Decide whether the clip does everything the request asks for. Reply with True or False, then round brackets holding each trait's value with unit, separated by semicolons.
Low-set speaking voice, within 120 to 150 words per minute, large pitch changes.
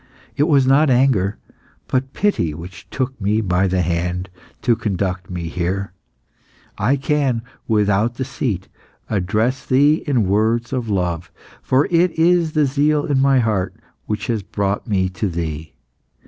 True (110 Hz; 145 wpm; 6.3 semitones)